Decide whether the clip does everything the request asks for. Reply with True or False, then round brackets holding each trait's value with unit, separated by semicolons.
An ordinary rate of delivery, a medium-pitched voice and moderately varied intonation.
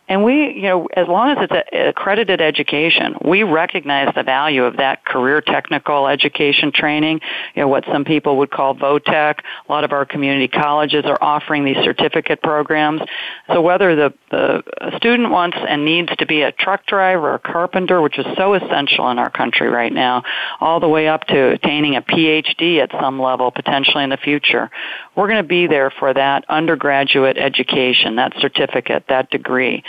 True (185 wpm; 150 Hz; 3.6 semitones)